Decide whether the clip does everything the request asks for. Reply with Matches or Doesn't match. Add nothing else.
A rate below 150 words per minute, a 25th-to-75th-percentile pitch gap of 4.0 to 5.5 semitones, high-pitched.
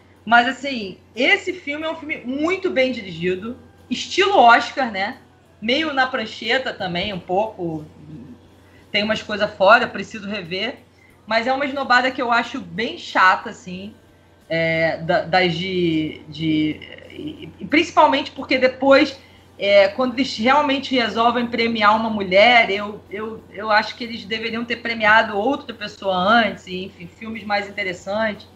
Matches